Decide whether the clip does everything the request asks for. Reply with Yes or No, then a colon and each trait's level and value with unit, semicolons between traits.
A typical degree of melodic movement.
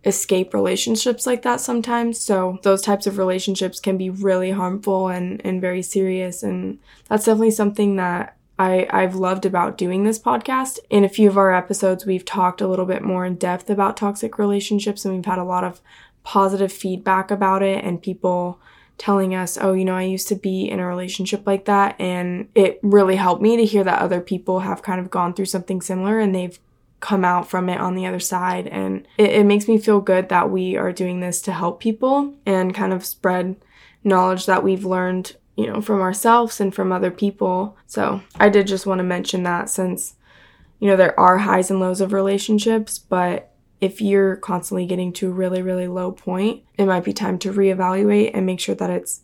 No: narrow, 1.7 semitones